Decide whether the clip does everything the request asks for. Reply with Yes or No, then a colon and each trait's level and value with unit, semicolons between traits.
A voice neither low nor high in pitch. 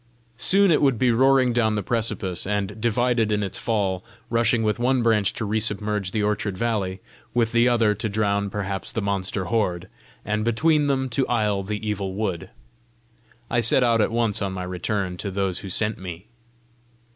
No: low, 105 Hz